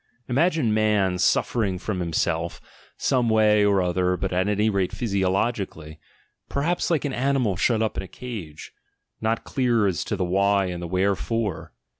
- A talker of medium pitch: No, low, 100 Hz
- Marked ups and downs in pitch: No, average, 3.9 semitones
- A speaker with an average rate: Yes, average, 165 wpm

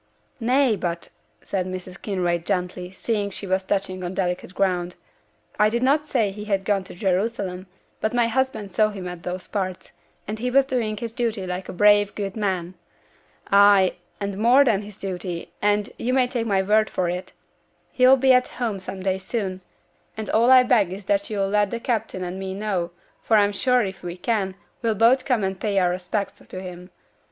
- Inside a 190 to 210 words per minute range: Yes, average, 200 wpm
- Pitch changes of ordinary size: Yes, average, 3.3 semitones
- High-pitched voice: Yes, high, 200 Hz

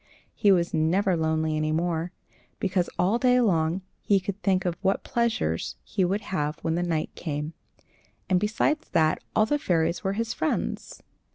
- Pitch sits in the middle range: Yes, medium, 180 Hz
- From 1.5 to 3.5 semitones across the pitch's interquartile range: No, average, 4.0 semitones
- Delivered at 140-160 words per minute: No, average, 170 wpm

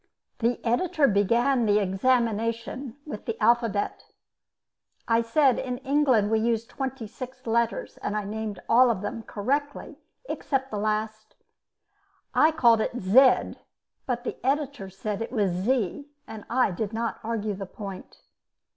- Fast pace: No, average, 145 wpm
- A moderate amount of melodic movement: Yes, average, 3.4 semitones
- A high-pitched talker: Yes, high, 230 Hz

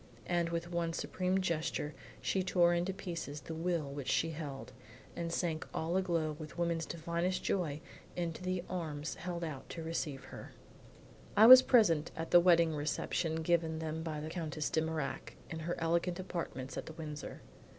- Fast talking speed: No, average, 170 wpm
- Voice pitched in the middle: Yes, medium, 165 Hz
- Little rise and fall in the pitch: Yes, narrow, 1.8 semitones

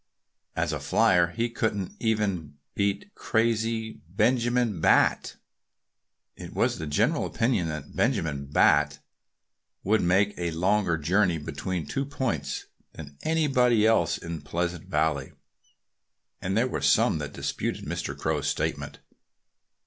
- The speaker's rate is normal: No, slow, 125 wpm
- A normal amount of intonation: No, wide, 6.1 semitones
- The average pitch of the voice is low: Yes, very low, 95 Hz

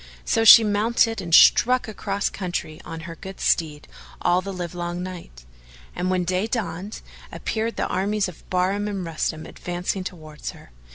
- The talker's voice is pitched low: No, medium, 185 Hz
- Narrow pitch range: No, average, 3.2 semitones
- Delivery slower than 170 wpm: Yes, average, 160 wpm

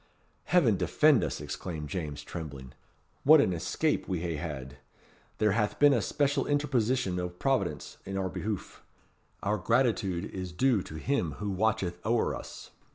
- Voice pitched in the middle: No, very low, 95 Hz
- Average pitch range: No, wide, 6.2 semitones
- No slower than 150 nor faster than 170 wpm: Yes, average, 155 wpm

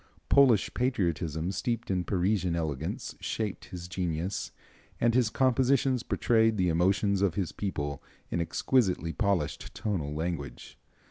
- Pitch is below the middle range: Yes, very low, 95 Hz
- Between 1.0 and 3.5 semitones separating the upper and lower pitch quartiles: No, average, 5.1 semitones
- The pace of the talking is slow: Yes, slow, 125 wpm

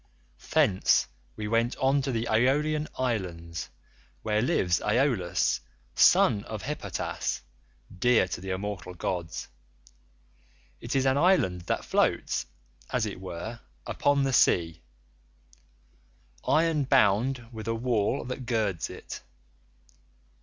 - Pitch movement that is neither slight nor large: No, wide, 6.6 semitones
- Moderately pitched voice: No, low, 105 Hz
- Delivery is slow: Yes, slow, 115 wpm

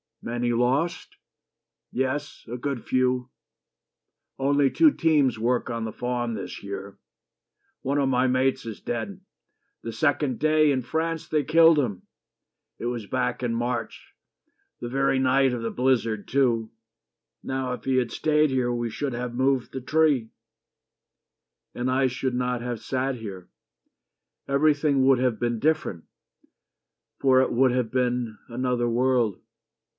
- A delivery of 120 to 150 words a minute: Yes, average, 140 wpm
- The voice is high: No, low, 125 Hz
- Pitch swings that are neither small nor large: No, narrow, 2.3 semitones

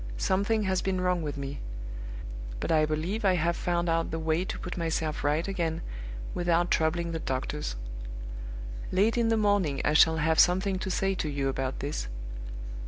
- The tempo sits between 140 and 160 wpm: No, average, 175 wpm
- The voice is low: No, medium, 170 Hz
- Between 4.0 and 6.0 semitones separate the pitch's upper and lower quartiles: No, average, 3.4 semitones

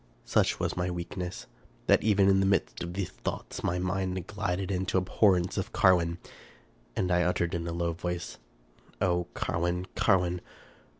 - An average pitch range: No, narrow, 1.4 semitones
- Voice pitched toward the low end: Yes, very low, 90 Hz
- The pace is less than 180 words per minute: Yes, average, 165 wpm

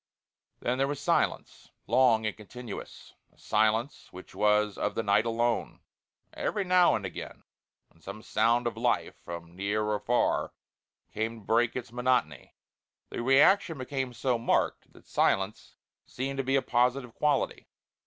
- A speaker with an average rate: Yes, average, 155 wpm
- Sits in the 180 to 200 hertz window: No, low, 120 Hz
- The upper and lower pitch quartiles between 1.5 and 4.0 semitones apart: Yes, average, 3.3 semitones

